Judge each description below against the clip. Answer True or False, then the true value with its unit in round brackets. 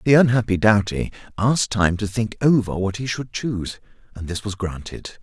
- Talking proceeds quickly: False (185 wpm)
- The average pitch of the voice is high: False (105 Hz)